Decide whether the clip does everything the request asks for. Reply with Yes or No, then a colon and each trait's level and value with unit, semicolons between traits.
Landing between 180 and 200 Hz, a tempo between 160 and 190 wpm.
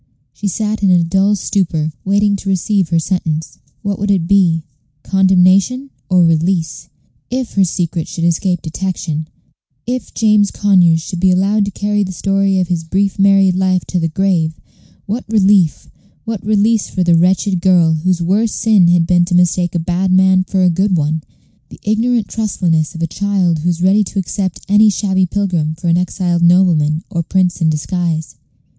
Yes: medium, 185 Hz; average, 180 wpm